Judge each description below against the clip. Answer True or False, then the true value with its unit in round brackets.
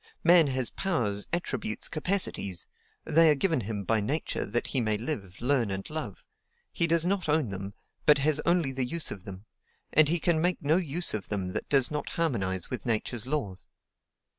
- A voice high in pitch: False (135 Hz)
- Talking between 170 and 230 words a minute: True (190 wpm)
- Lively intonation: True (7.8 semitones)